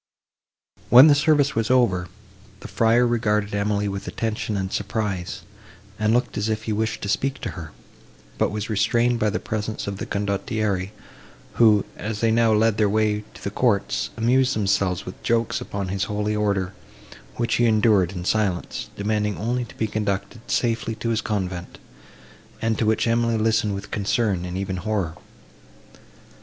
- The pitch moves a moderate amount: No, narrow, 2.3 semitones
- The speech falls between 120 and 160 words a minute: No, average, 170 wpm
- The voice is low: Yes, low, 105 Hz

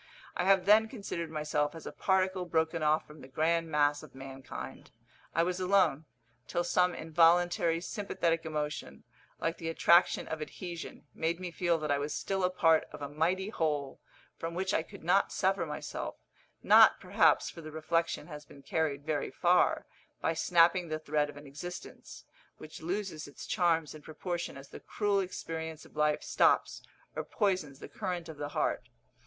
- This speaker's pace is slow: No, average, 175 wpm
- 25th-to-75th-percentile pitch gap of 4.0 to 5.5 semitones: No, average, 2.9 semitones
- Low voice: No, medium, 165 Hz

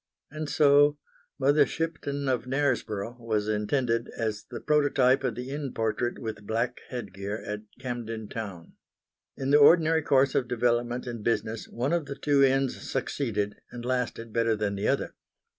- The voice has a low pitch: Yes, low, 125 Hz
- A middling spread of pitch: Yes, average, 3.9 semitones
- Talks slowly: No, average, 160 wpm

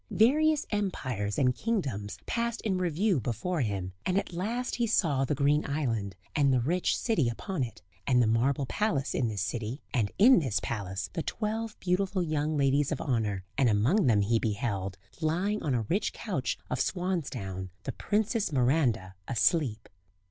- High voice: No, medium, 140 Hz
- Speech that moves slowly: No, average, 170 wpm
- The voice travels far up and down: Yes, wide, 8.7 semitones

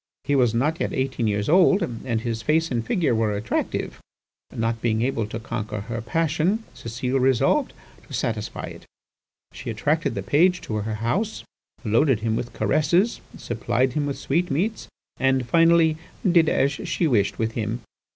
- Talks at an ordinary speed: Yes, average, 160 wpm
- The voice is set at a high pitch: No, low, 125 Hz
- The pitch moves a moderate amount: No, wide, 5.9 semitones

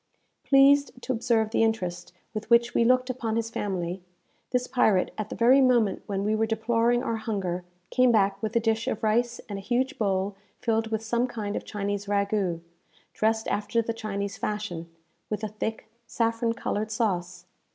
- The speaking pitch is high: Yes, high, 220 Hz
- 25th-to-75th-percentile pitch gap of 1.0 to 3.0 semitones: Yes, narrow, 2.6 semitones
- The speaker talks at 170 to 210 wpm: Yes, average, 180 wpm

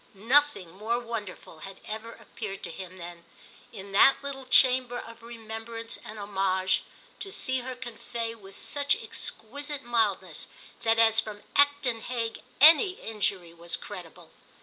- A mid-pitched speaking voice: No, high, 225 Hz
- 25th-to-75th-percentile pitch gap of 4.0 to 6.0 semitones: Yes, average, 4.3 semitones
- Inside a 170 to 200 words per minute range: No, average, 140 wpm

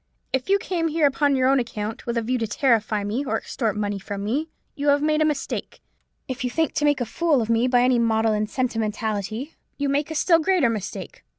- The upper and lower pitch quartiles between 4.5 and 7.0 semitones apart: Yes, average, 4.8 semitones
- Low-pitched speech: No, very high, 250 Hz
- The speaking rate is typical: No, fast, 230 wpm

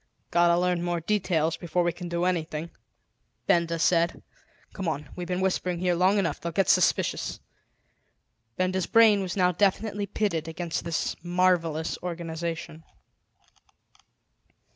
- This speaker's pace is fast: No, slow, 135 wpm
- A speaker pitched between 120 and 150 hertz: No, medium, 175 Hz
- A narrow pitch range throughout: Yes, narrow, 1.7 semitones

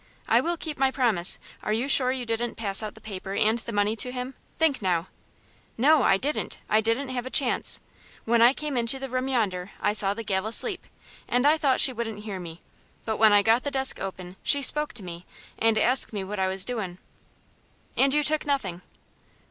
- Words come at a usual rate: No, fast, 215 wpm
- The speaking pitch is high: Yes, high, 230 Hz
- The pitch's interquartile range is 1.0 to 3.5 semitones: No, average, 4.7 semitones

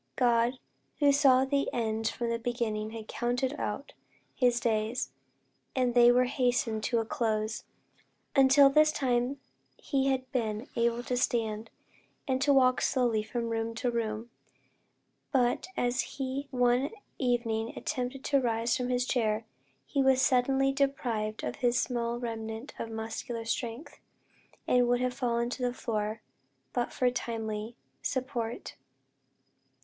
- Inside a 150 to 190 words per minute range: No, average, 140 wpm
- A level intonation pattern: Yes, narrow, 2.3 semitones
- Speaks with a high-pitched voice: Yes, high, 245 Hz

